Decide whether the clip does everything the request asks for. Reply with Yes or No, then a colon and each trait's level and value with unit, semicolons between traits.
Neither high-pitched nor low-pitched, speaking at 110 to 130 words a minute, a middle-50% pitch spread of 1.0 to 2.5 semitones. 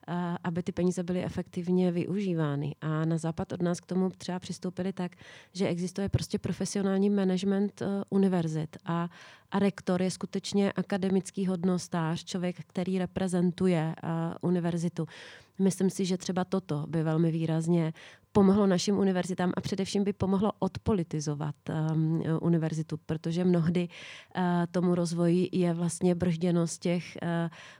Yes: medium, 180 Hz; average, 125 wpm; narrow, 2.2 semitones